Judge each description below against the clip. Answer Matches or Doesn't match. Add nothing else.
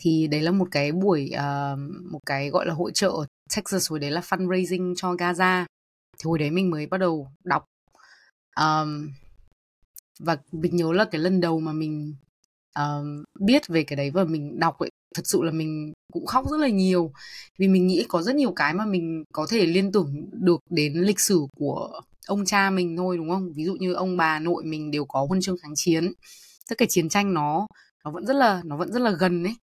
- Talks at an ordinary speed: Matches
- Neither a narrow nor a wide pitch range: Matches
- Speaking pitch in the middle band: Matches